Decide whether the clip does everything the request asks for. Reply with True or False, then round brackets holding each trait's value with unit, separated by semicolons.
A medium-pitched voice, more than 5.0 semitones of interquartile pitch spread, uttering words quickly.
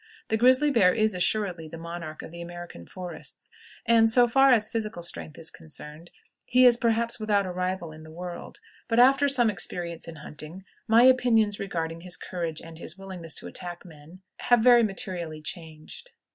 False (180 Hz; 5.5 semitones; 180 wpm)